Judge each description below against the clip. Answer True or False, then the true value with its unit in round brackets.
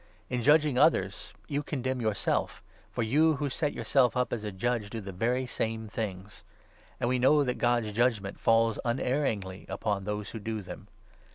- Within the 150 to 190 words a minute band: True (180 wpm)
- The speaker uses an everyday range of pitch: True (3.7 semitones)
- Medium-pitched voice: False (115 Hz)